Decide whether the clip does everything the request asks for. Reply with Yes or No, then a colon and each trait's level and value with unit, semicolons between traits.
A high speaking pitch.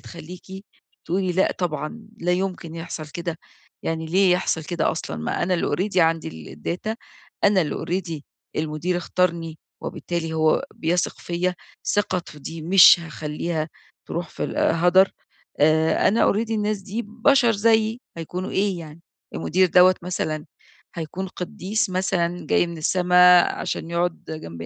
No: medium, 175 Hz